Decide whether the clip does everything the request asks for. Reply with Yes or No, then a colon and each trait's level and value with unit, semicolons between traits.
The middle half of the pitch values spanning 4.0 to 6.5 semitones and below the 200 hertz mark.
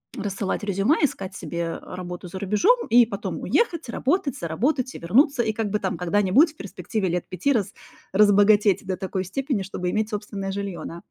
No: average, 4.3 semitones; high, 205 Hz